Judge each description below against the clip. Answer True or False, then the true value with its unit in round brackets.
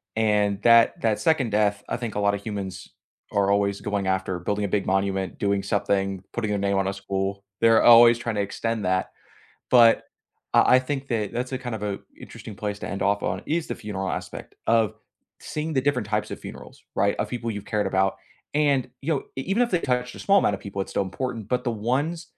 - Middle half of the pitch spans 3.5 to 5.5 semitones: True (3.8 semitones)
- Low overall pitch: True (105 Hz)